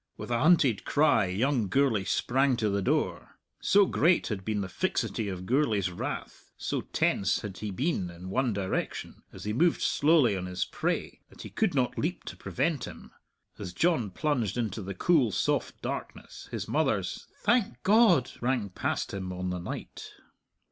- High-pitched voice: No, low, 115 Hz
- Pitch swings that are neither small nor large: No, wide, 7.1 semitones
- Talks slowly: No, average, 175 wpm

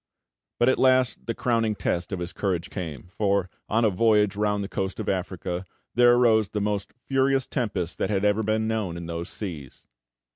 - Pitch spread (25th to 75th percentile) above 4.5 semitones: No, average, 3.7 semitones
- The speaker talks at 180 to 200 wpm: Yes, average, 190 wpm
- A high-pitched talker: No, low, 105 Hz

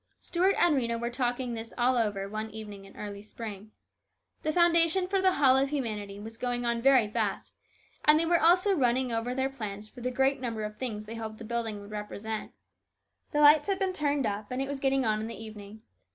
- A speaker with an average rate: No, fast, 220 wpm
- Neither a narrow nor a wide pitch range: Yes, average, 4.3 semitones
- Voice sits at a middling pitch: No, high, 235 Hz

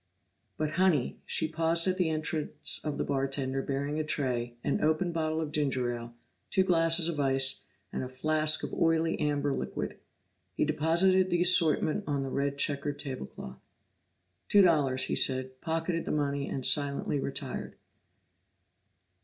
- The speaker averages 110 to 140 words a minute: No, average, 160 wpm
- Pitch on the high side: No, medium, 150 Hz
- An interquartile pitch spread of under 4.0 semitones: Yes, average, 3.2 semitones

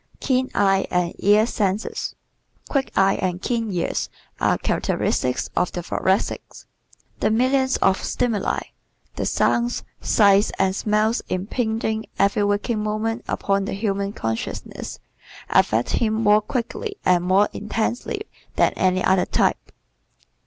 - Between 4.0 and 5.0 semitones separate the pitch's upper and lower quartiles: No, average, 2.9 semitones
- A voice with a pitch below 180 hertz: No, high, 210 Hz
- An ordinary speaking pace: No, slow, 130 wpm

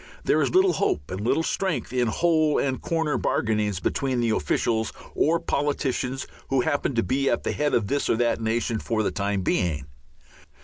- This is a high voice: No, low, 125 Hz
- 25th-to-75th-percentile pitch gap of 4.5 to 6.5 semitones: Yes, average, 5.1 semitones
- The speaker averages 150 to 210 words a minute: Yes, average, 185 wpm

